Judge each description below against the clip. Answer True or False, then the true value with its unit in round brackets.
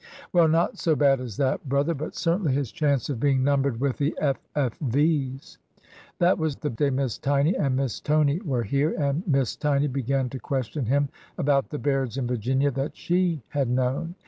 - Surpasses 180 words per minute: True (200 wpm)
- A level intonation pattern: True (2.2 semitones)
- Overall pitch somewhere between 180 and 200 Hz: False (140 Hz)